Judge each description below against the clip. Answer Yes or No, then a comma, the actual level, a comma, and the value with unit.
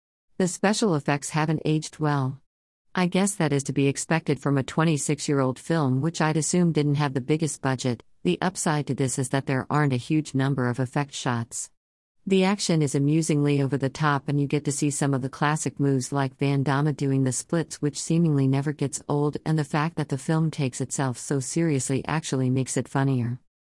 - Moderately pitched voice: Yes, medium, 145 Hz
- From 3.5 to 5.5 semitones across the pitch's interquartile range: No, narrow, 2.6 semitones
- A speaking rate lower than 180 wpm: No, fast, 205 wpm